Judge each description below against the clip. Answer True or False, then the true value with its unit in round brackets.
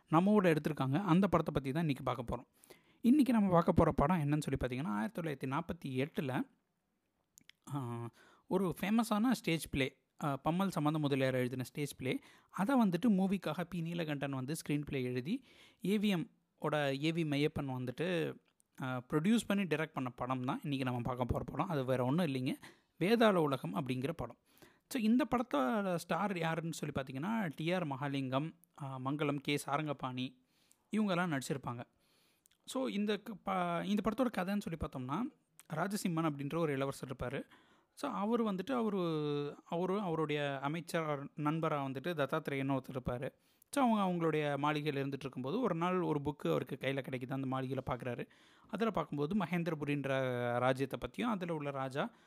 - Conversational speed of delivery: False (145 wpm)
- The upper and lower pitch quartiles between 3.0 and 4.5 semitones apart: False (5.3 semitones)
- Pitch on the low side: False (155 Hz)